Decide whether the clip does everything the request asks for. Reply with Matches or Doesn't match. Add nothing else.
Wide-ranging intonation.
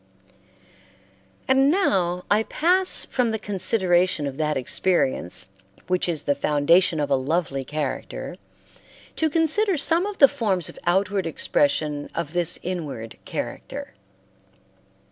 Matches